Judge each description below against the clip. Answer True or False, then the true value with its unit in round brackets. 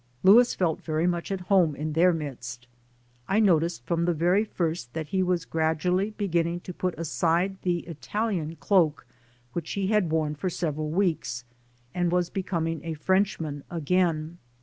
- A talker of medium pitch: True (170 Hz)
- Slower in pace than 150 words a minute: False (165 wpm)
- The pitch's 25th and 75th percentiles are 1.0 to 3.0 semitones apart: True (2.7 semitones)